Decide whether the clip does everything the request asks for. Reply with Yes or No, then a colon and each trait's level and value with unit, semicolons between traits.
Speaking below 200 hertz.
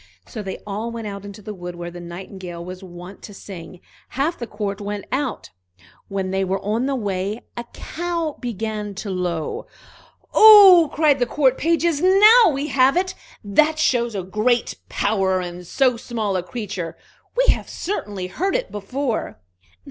No: high, 215 Hz